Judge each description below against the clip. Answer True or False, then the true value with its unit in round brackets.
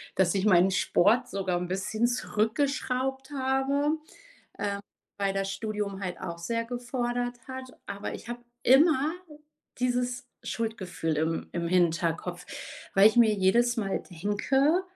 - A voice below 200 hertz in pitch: False (220 Hz)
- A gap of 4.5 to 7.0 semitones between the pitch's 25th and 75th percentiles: True (4.9 semitones)